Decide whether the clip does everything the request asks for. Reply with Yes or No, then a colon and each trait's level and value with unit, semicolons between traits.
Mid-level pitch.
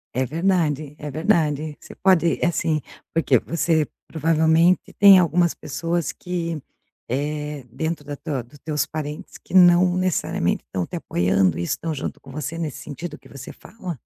Yes: medium, 155 Hz